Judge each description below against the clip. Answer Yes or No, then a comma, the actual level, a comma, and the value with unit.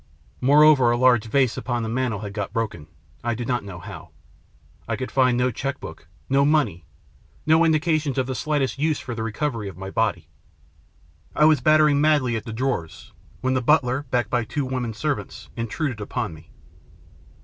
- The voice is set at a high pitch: No, low, 125 Hz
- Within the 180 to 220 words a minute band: Yes, average, 185 wpm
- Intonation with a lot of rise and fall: No, average, 4.3 semitones